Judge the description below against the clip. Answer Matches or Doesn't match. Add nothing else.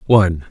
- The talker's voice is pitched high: Doesn't match